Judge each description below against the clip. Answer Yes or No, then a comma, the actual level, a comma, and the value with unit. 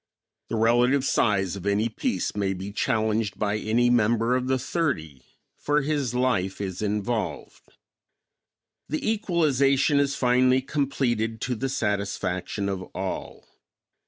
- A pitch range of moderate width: Yes, average, 4.7 semitones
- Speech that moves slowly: Yes, slow, 130 wpm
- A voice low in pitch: Yes, low, 115 Hz